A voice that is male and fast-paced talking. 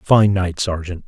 No: male; average, 170 wpm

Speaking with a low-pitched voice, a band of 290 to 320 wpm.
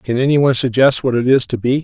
Yes: low, 125 Hz; fast, 295 wpm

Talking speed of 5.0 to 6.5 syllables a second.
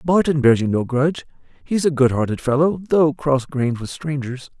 Yes: 5.2 syllables/s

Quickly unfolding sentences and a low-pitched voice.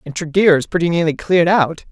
No: fast, 220 wpm; medium, 165 Hz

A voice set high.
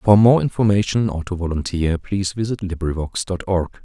No: very low, 95 Hz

